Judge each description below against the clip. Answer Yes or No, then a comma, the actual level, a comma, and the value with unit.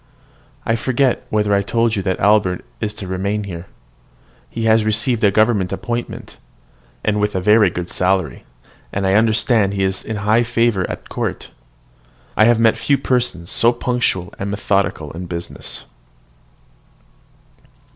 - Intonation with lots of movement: No, average, 3.2 semitones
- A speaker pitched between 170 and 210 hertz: No, low, 105 Hz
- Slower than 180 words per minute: Yes, average, 145 wpm